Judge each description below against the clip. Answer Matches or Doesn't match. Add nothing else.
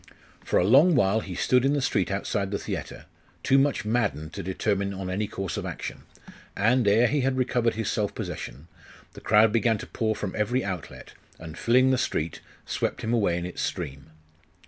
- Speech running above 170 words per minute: Matches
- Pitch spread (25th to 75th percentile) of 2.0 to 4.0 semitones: Doesn't match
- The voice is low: Matches